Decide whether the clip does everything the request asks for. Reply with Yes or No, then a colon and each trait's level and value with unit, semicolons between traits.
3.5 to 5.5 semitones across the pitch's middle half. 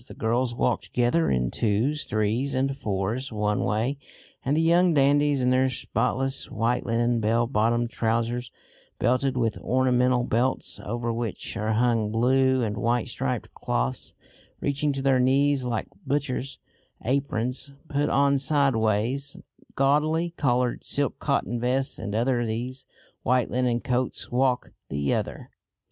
No: average, 2.9 semitones